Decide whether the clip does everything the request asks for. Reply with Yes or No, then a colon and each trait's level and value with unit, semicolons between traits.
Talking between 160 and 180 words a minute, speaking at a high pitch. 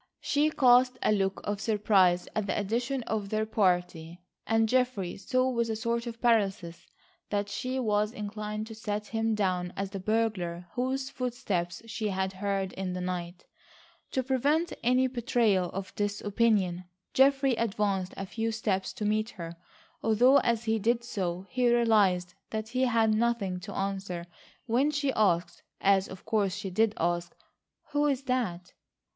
Yes: average, 165 wpm; high, 215 Hz